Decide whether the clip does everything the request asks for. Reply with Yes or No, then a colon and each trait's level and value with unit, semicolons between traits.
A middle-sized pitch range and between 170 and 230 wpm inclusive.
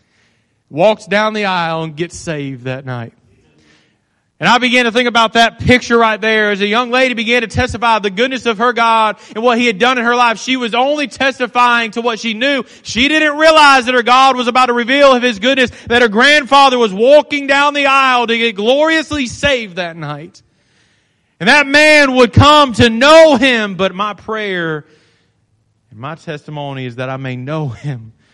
No: wide, 8.0 semitones; average, 200 wpm